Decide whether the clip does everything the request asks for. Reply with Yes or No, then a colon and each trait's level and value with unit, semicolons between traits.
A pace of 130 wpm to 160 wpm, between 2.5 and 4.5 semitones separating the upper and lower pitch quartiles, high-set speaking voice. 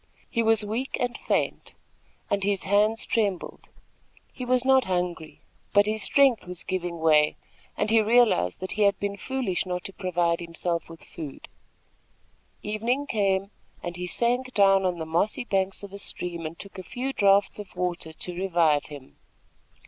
No: average, 170 wpm; average, 4.0 semitones; high, 195 Hz